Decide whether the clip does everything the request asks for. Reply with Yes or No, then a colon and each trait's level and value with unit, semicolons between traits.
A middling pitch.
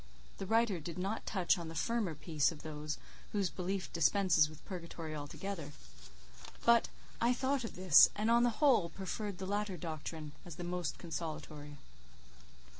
Yes: medium, 180 Hz